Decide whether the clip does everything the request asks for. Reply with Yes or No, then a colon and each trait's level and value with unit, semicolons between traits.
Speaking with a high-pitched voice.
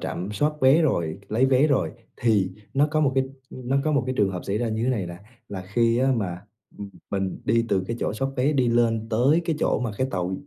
No: low, 115 Hz